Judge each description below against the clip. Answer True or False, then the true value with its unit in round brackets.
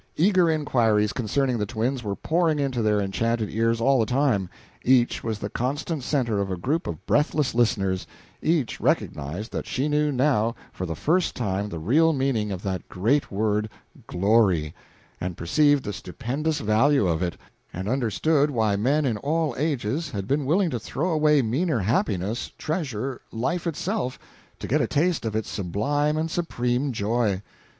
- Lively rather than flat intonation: True (6.0 semitones)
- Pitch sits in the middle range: False (120 Hz)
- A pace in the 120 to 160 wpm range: False (170 wpm)